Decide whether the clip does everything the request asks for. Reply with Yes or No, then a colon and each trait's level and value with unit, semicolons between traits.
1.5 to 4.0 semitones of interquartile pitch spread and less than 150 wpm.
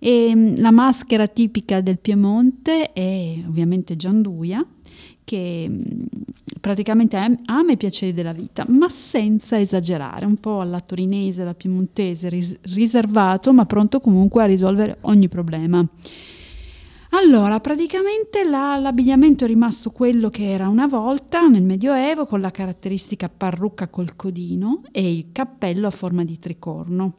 No: average, 4.8 semitones; average, 130 wpm